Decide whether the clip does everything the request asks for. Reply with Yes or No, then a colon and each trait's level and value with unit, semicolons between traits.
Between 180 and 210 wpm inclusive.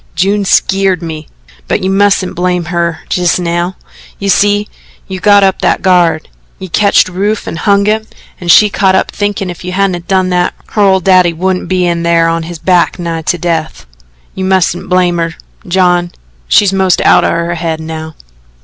Yes: average, 185 wpm